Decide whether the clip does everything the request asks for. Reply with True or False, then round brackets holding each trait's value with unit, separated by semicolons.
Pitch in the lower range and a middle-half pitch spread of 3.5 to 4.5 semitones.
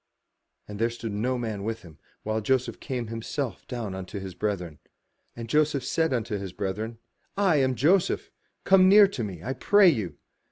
False (115 Hz; 5.1 semitones)